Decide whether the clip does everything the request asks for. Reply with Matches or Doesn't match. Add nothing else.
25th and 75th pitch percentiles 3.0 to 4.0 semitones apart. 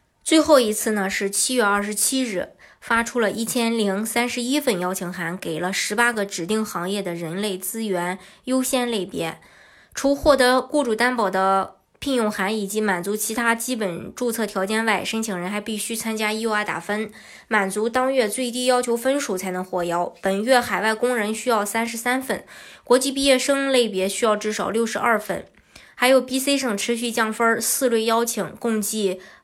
Matches